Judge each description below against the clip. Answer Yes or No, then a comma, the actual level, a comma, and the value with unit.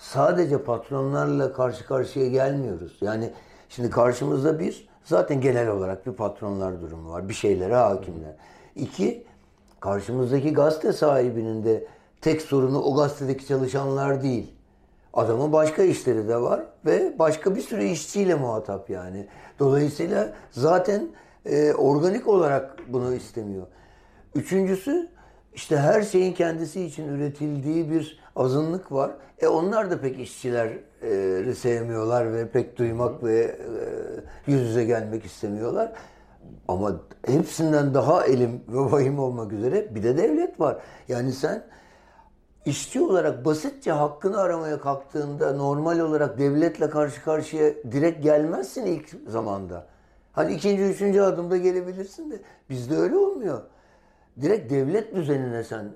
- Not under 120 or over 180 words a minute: Yes, average, 125 wpm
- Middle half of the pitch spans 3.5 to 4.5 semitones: No, average, 5.3 semitones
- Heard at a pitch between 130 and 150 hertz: Yes, medium, 140 Hz